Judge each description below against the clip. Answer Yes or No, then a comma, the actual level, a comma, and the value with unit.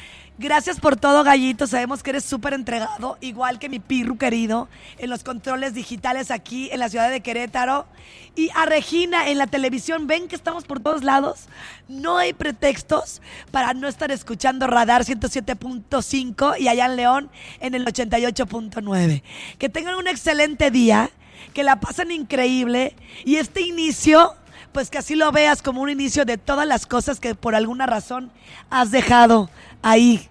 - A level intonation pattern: No, average, 3.0 semitones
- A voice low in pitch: No, very high, 265 Hz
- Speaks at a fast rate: No, average, 165 wpm